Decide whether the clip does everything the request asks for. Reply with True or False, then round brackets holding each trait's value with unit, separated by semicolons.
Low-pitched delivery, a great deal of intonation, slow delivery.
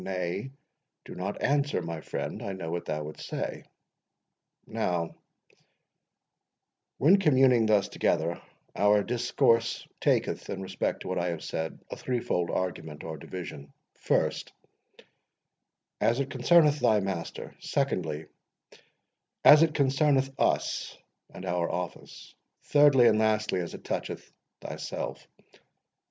True (100 Hz; 7.6 semitones; 120 wpm)